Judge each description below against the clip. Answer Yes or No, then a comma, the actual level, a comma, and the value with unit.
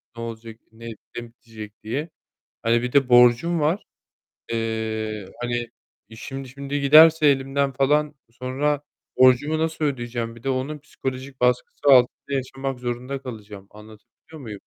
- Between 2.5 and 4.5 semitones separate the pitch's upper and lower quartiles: Yes, average, 3.3 semitones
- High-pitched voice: No, low, 125 Hz